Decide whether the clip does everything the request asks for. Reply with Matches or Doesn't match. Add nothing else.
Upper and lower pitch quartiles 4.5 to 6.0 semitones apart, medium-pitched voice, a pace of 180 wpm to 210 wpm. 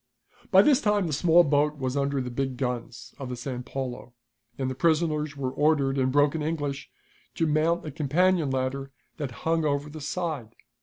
Doesn't match